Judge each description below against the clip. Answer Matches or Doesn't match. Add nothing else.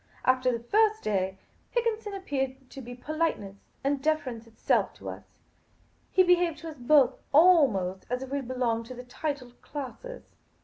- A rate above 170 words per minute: Doesn't match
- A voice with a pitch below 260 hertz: Doesn't match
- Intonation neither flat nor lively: Matches